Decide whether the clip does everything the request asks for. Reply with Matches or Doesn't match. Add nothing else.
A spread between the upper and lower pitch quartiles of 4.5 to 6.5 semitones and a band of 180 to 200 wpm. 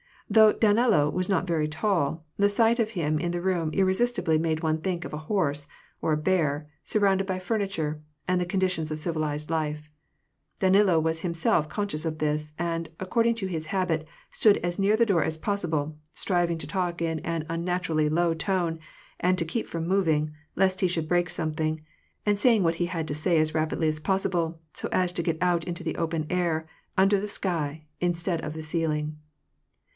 Doesn't match